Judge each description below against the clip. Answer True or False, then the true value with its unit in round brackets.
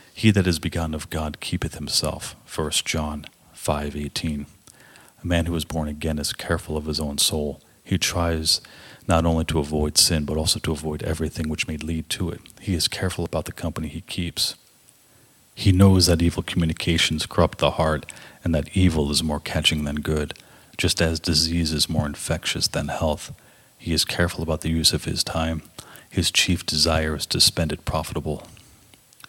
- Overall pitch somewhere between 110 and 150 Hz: False (80 Hz)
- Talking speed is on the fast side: False (185 wpm)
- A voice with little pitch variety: True (2.0 semitones)